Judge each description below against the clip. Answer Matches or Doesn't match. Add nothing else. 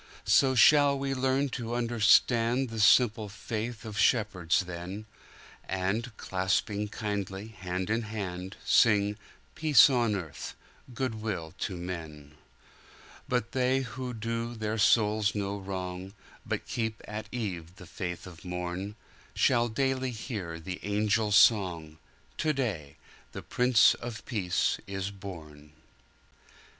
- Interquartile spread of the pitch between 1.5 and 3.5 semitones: Doesn't match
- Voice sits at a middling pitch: Doesn't match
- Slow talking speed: Matches